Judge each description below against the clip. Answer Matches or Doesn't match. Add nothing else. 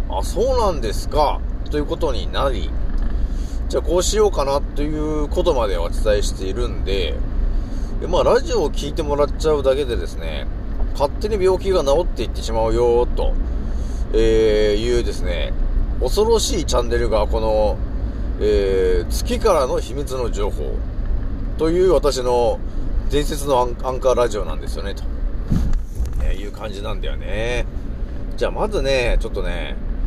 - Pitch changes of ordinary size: Doesn't match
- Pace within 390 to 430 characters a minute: Doesn't match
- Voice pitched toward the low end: Matches